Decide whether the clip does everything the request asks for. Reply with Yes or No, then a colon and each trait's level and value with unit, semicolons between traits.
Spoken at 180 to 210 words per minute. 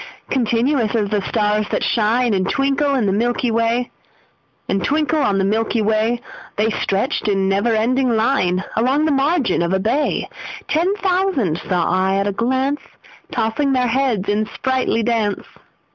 No: average, 140 wpm